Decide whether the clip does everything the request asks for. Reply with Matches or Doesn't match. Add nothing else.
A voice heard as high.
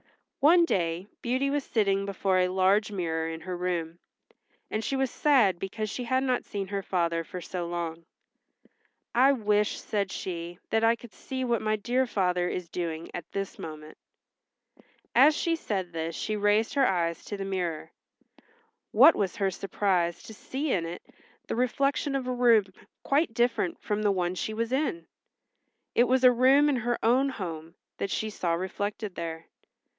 Matches